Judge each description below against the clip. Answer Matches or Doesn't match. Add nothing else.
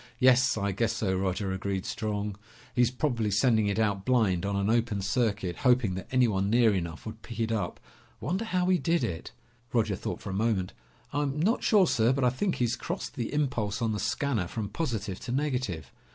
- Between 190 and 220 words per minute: Matches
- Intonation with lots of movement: Doesn't match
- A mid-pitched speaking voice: Doesn't match